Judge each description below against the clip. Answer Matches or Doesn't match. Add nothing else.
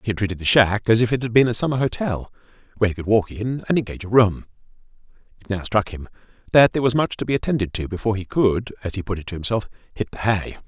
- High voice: Doesn't match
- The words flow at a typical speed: Doesn't match